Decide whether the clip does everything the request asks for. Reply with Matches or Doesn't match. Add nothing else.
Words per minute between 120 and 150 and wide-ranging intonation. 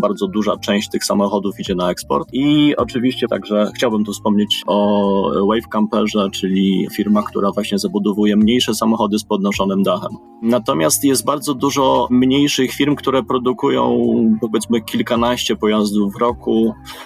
Doesn't match